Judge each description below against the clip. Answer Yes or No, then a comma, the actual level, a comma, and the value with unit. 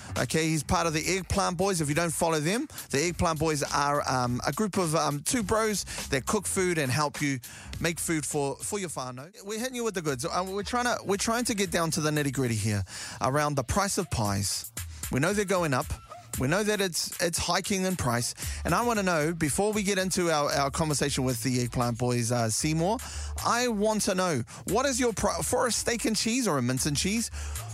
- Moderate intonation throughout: No, wide, 7.4 semitones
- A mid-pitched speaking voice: Yes, medium, 160 Hz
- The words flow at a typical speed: No, fast, 235 wpm